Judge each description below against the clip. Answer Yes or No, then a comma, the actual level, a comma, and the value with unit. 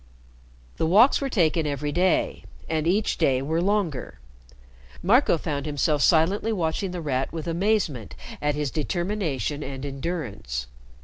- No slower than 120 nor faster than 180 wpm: Yes, average, 140 wpm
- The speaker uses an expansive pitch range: No, average, 4.6 semitones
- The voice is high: No, medium, 160 Hz